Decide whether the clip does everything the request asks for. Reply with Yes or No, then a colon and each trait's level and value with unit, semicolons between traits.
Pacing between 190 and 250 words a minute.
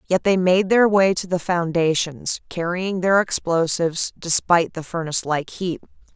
No: average, 155 wpm